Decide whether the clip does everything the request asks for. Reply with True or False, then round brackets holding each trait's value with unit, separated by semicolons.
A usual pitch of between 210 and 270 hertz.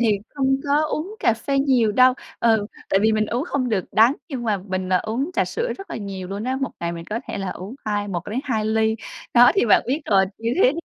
True (225 Hz)